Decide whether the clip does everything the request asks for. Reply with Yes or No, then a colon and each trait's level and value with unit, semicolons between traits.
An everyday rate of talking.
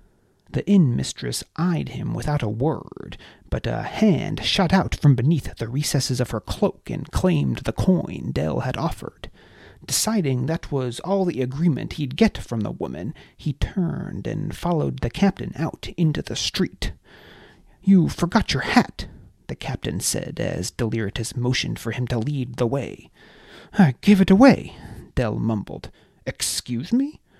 Yes: average, 160 wpm